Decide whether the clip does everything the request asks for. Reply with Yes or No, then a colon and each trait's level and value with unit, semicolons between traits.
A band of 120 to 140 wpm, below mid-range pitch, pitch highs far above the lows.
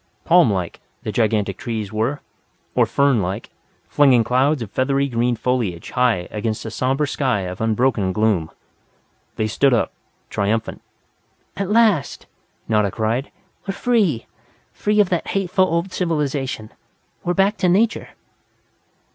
Yes: slow, 135 wpm; low, 125 Hz; wide, 7.1 semitones